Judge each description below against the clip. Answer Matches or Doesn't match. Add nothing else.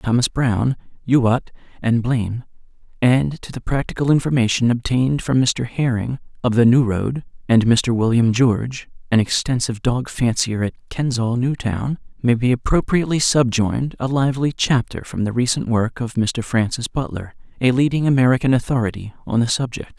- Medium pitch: Doesn't match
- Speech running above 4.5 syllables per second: Matches